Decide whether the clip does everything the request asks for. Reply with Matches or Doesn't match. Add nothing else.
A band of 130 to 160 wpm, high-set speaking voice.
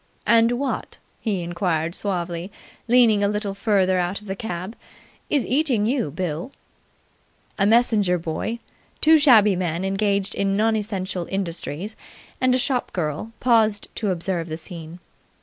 Matches